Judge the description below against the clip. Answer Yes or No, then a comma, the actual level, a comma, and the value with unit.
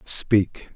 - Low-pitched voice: Yes, low, 100 Hz